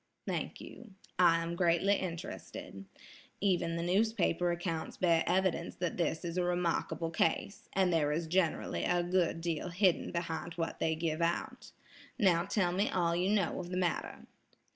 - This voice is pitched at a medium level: Yes, medium, 175 Hz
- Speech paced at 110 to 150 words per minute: No, average, 165 wpm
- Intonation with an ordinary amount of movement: No, narrow, 1.7 semitones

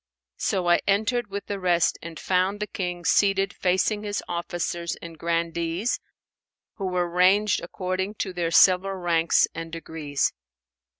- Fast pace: No, average, 140 wpm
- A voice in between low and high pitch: Yes, medium, 180 Hz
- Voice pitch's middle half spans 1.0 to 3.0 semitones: Yes, narrow, 2.5 semitones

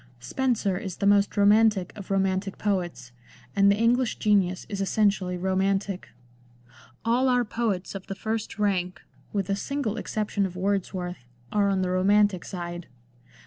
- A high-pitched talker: Yes, high, 200 Hz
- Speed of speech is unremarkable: Yes, average, 150 wpm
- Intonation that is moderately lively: No, narrow, 2.3 semitones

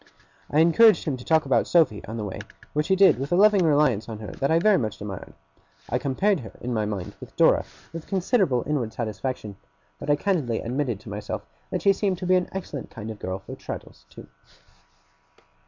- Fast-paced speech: Yes, fast, 210 wpm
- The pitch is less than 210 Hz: Yes, medium, 140 Hz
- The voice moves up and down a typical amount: No, wide, 8.0 semitones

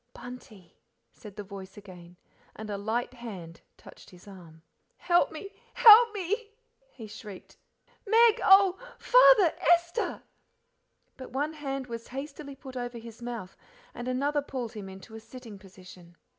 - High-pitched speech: Yes, high, 245 Hz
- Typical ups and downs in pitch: No, wide, 7.5 semitones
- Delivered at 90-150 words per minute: Yes, average, 145 wpm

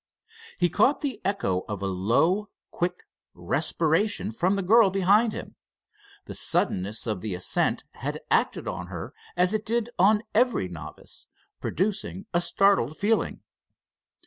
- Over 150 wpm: No, average, 140 wpm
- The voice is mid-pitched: Yes, medium, 180 Hz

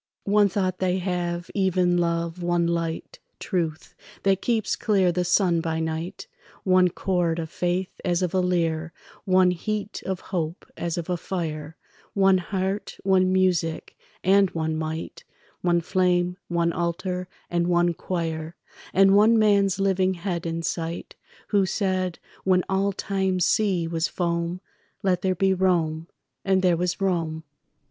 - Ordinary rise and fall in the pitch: No, narrow, 2.0 semitones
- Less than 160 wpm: Yes, average, 145 wpm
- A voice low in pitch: No, medium, 180 Hz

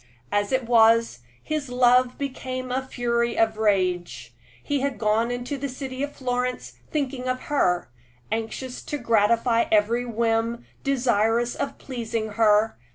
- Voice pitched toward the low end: No, high, 235 Hz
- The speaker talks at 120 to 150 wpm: Yes, average, 140 wpm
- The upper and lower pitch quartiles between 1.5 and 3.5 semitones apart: Yes, narrow, 2.6 semitones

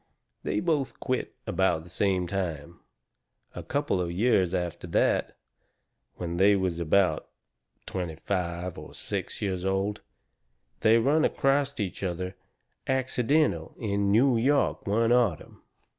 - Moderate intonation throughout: No, wide, 5.7 semitones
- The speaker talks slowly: Yes, slow, 130 wpm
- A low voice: Yes, low, 100 Hz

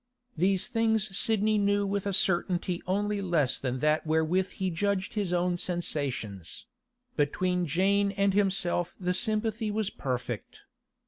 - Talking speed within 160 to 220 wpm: No, slow, 135 wpm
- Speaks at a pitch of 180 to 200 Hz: Yes, medium, 185 Hz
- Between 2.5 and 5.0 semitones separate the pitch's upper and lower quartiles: Yes, average, 2.9 semitones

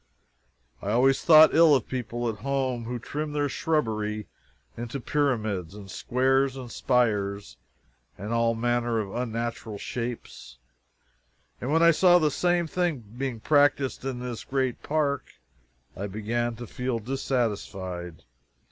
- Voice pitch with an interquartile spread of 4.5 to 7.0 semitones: No, average, 4.0 semitones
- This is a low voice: Yes, low, 120 Hz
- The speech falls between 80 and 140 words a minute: Yes, slow, 135 wpm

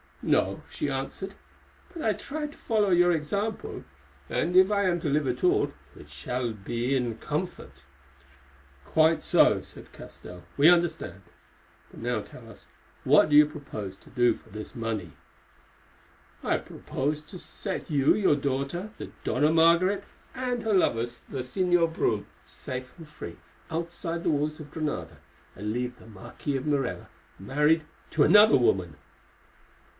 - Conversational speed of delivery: Yes, average, 155 wpm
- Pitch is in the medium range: Yes, medium, 150 Hz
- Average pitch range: No, wide, 6.2 semitones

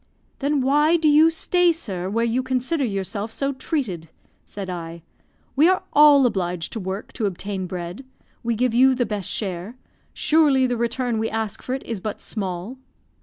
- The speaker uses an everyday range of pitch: No, wide, 6.1 semitones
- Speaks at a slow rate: No, average, 175 wpm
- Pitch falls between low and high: No, high, 235 Hz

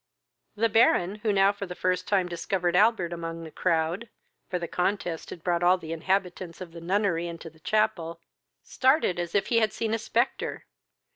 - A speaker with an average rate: Yes, average, 190 wpm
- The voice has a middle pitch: Yes, medium, 180 Hz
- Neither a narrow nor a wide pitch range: Yes, average, 3.3 semitones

